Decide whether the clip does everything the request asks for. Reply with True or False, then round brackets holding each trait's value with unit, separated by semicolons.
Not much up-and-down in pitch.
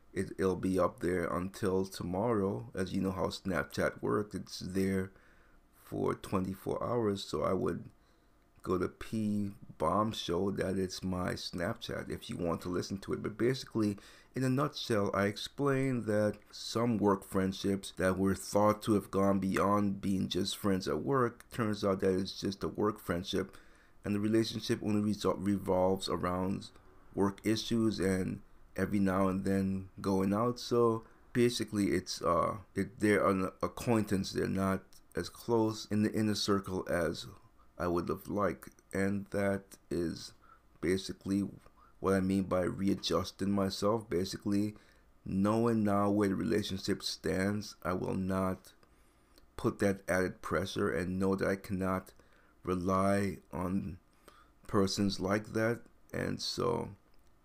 True (1.9 semitones)